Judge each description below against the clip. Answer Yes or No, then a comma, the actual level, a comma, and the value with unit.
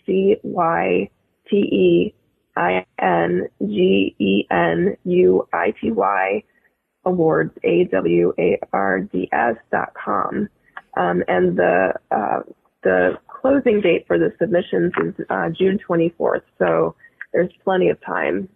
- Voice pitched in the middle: Yes, medium, 165 Hz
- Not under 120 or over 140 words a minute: Yes, slow, 135 wpm